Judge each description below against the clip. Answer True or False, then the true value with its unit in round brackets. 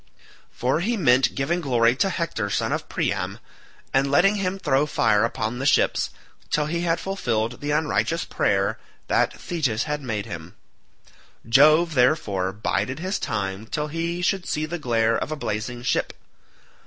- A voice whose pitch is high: False (135 Hz)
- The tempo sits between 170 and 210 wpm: False (160 wpm)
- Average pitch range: False (6.7 semitones)